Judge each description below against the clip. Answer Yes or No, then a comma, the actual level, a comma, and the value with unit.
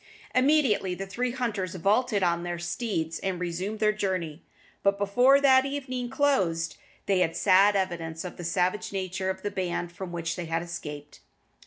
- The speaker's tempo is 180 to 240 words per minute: No, average, 170 wpm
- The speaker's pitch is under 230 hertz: Yes, high, 190 Hz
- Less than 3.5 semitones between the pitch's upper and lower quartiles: No, average, 4.0 semitones